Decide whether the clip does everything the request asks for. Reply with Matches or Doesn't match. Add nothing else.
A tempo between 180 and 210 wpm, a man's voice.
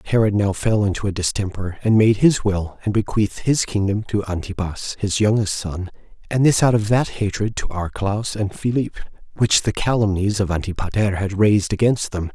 Matches